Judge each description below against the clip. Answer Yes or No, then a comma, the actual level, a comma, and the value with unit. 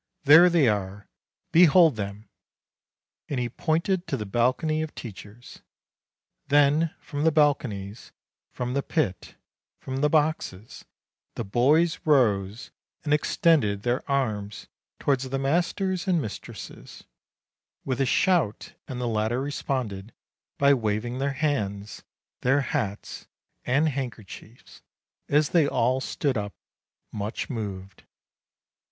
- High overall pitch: No, low, 130 Hz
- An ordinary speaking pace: No, slow, 120 wpm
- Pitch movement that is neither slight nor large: No, wide, 5.8 semitones